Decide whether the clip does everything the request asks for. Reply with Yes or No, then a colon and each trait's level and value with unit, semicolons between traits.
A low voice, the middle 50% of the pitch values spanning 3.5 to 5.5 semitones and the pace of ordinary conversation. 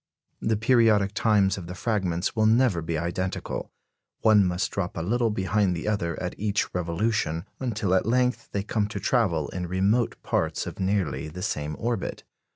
Yes: low, 100 Hz; average, 3.8 semitones; average, 170 wpm